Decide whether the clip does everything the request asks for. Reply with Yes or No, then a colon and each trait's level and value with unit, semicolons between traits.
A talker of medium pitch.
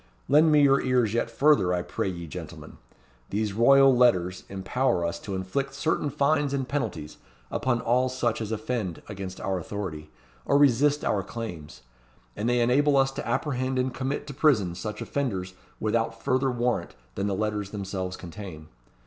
No: low, 115 Hz